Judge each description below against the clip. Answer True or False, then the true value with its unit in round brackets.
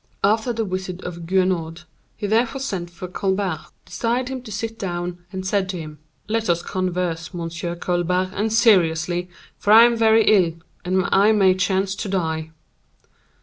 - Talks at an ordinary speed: True (165 wpm)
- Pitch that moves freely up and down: False (3.6 semitones)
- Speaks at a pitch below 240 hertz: True (185 Hz)